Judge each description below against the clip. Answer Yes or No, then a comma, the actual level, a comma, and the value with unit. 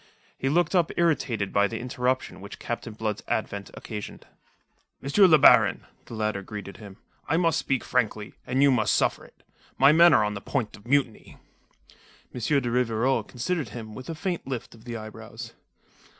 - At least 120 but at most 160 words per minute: No, average, 180 wpm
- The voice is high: No, low, 120 Hz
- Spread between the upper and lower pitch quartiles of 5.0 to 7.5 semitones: No, average, 4.6 semitones